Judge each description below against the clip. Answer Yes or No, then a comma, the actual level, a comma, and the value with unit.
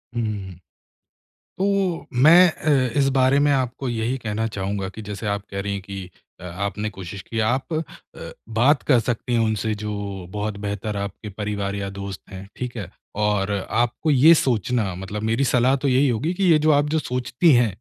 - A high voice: No, low, 110 Hz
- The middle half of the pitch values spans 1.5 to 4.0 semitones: No, average, 4.6 semitones